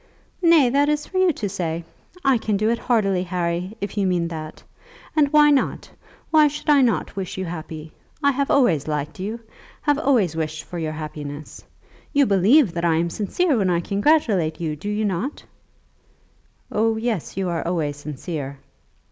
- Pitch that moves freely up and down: Yes, wide, 8.1 semitones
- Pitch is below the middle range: No, high, 195 Hz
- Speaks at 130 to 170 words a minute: No, average, 180 wpm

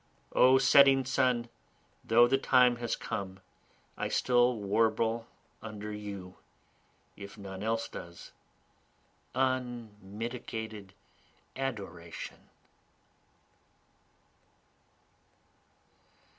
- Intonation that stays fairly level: No, average, 3.5 semitones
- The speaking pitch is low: Yes, low, 115 Hz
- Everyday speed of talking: No, slow, 70 wpm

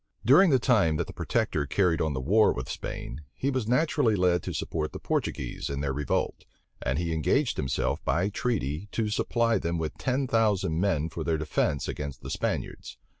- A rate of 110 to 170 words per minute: No, average, 190 wpm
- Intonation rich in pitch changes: Yes, wide, 6.8 semitones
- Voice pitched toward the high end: No, very low, 85 Hz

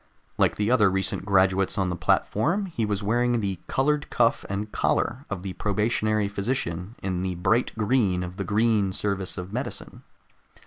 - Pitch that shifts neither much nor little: Yes, average, 3.5 semitones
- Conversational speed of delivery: Yes, average, 170 wpm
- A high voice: No, low, 105 Hz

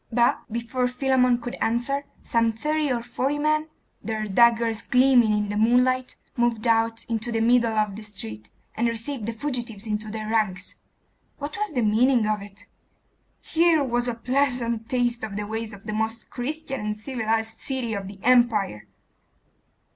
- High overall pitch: Yes, high, 230 Hz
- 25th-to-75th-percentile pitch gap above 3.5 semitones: No, narrow, 2.6 semitones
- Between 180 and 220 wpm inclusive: No, average, 165 wpm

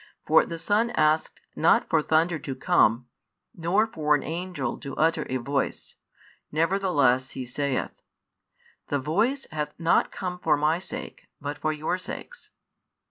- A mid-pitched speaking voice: Yes, medium, 155 Hz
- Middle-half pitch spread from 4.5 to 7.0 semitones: No, average, 4.0 semitones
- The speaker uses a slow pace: No, average, 145 wpm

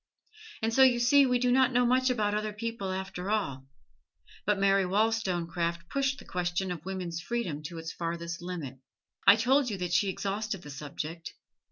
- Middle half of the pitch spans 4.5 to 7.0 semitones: Yes, average, 5.2 semitones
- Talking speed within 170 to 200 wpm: Yes, average, 180 wpm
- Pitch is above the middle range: Yes, high, 195 Hz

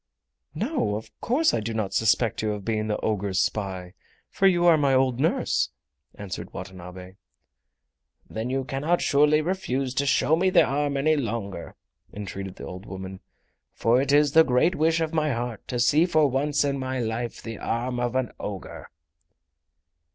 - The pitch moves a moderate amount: No, wide, 6.0 semitones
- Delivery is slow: No, average, 175 wpm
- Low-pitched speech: Yes, low, 125 Hz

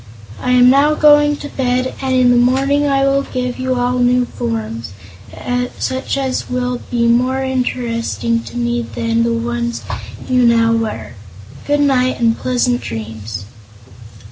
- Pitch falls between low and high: No, high, 245 Hz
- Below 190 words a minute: Yes, average, 150 wpm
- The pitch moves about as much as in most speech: No, narrow, 2.1 semitones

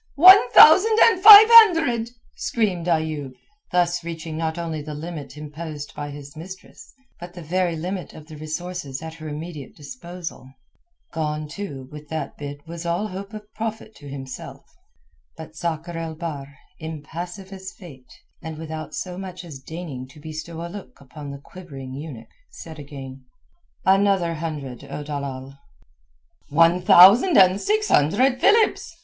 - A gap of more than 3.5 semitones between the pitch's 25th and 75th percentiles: Yes, average, 4.0 semitones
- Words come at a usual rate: Yes, average, 150 wpm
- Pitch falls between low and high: Yes, medium, 165 Hz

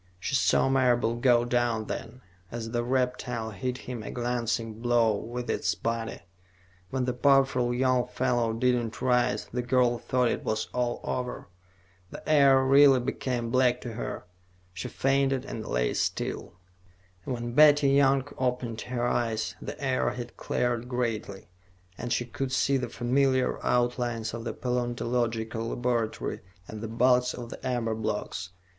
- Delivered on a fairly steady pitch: Yes, narrow, 1.7 semitones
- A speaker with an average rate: Yes, average, 150 wpm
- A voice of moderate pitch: No, low, 120 Hz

